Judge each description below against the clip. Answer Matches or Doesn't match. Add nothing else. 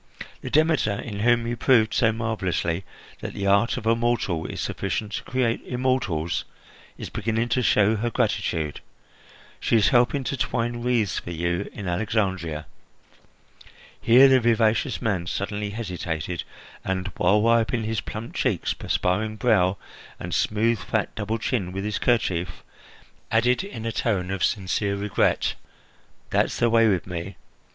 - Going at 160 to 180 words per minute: Doesn't match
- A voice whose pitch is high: Doesn't match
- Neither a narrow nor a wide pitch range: Matches